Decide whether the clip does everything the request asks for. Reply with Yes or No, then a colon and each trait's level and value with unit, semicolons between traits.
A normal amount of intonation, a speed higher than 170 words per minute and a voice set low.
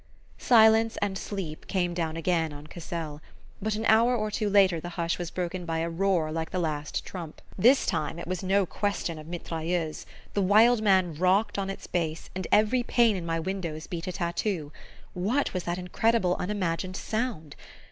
No: average, 3.7 semitones; average, 185 wpm; medium, 180 Hz